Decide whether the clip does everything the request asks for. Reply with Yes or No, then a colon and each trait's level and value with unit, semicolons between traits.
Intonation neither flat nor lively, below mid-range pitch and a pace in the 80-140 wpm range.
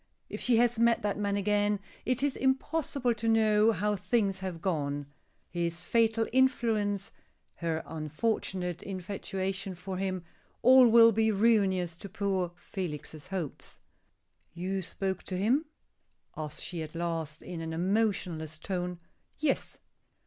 No: average, 4.3 semitones; high, 195 Hz; slow, 135 wpm